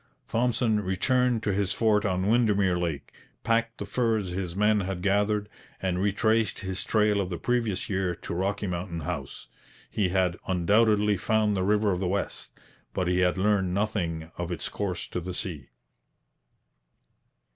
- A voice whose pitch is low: Yes, low, 100 Hz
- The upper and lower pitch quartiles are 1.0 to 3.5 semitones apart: Yes, average, 2.9 semitones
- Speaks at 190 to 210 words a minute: No, average, 160 wpm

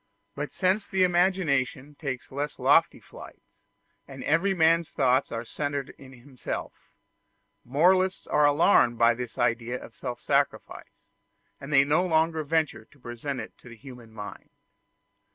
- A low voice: No, medium, 145 Hz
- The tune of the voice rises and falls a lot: No, average, 4.8 semitones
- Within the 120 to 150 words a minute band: Yes, average, 145 wpm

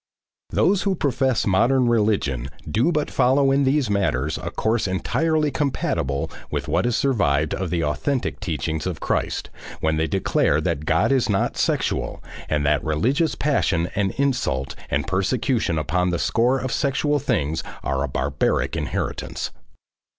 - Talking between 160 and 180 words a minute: No, average, 150 wpm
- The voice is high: No, low, 105 Hz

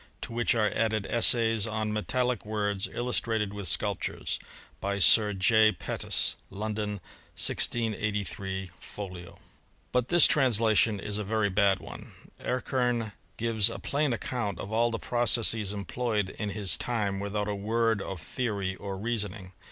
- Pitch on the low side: Yes, low, 105 Hz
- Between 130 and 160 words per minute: Yes, average, 145 wpm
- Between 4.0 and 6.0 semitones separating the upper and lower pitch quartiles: No, narrow, 2.5 semitones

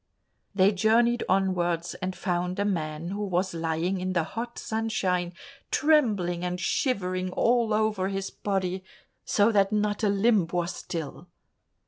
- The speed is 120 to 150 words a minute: Yes, average, 140 wpm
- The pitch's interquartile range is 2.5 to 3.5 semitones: Yes, average, 3.0 semitones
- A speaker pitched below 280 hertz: Yes, high, 190 Hz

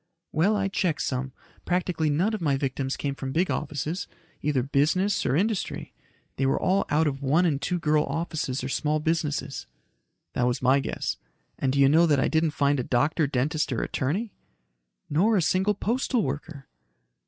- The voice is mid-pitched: Yes, medium, 150 Hz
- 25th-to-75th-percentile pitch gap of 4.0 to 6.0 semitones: Yes, average, 4.5 semitones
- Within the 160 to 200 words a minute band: Yes, average, 180 wpm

